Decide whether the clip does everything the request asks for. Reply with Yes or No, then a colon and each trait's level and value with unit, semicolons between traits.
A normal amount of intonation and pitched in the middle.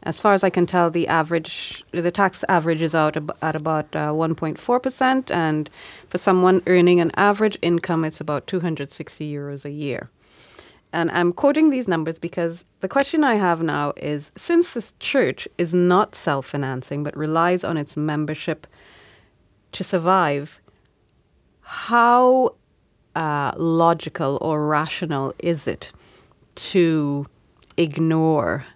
Yes: average, 3.2 semitones; medium, 165 Hz